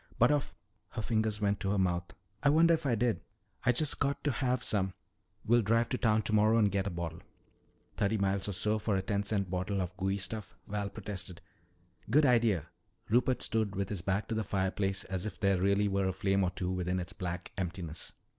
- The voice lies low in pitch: Yes, low, 100 Hz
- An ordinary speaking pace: No, fast, 215 wpm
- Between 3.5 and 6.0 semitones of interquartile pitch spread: No, average, 2.9 semitones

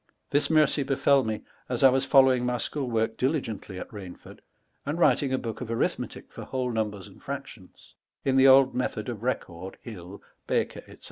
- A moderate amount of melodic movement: Yes, average, 3.4 semitones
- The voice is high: No, low, 125 Hz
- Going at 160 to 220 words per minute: Yes, average, 185 wpm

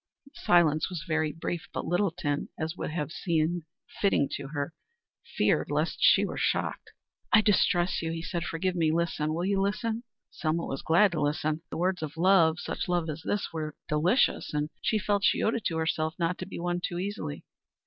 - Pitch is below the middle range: No, medium, 170 Hz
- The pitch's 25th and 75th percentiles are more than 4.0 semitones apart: No, average, 3.0 semitones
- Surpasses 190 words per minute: Yes, average, 200 wpm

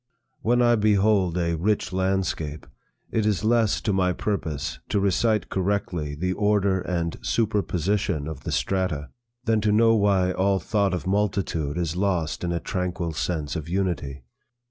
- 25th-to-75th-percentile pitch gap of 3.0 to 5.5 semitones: Yes, average, 3.5 semitones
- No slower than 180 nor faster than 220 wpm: No, average, 155 wpm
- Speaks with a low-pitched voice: Yes, very low, 95 Hz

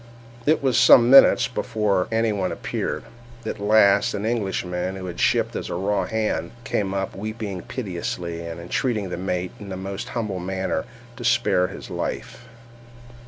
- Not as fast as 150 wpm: No, average, 160 wpm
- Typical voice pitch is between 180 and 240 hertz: No, low, 100 Hz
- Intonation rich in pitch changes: No, average, 3.5 semitones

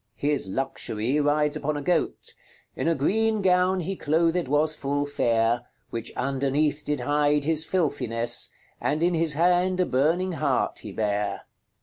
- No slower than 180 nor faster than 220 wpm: No, average, 150 wpm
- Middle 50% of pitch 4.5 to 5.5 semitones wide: No, average, 3.9 semitones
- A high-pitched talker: No, medium, 150 Hz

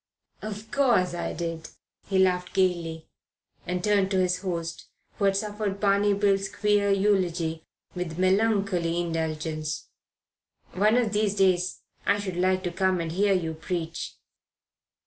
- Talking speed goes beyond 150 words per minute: No, average, 140 wpm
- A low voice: No, medium, 185 Hz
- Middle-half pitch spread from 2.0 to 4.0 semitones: Yes, average, 2.9 semitones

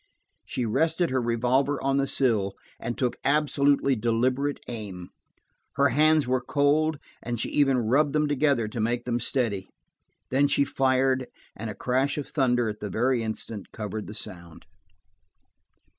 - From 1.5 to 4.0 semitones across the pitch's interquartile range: Yes, average, 3.7 semitones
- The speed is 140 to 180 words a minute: Yes, average, 155 wpm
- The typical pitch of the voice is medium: No, low, 130 Hz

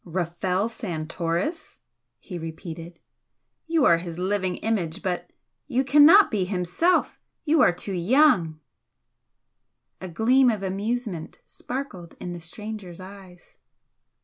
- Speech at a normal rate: No, slow, 115 wpm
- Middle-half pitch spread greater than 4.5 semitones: Yes, average, 5.1 semitones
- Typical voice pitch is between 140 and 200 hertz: Yes, medium, 185 Hz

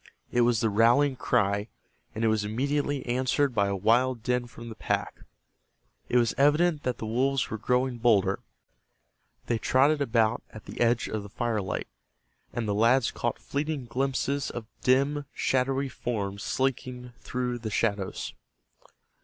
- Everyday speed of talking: Yes, average, 155 wpm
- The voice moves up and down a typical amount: Yes, average, 3.1 semitones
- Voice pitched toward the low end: Yes, low, 120 Hz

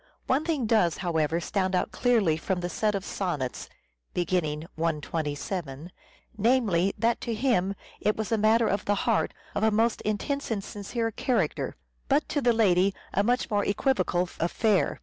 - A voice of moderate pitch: No, high, 205 Hz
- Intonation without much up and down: No, average, 4.6 semitones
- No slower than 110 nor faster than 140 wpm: No, average, 165 wpm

